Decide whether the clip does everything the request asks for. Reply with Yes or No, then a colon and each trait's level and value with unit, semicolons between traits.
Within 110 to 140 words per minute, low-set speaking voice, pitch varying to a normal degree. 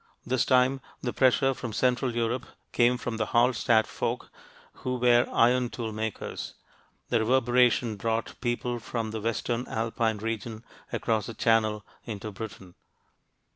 No: slow, 135 wpm; low, 115 Hz; narrow, 1.9 semitones